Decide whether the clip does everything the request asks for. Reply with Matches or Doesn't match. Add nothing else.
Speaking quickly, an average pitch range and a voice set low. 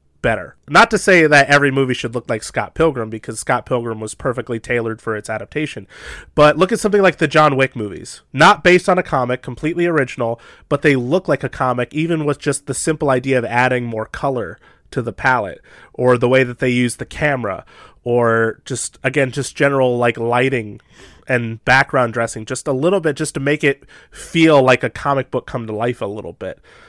Matches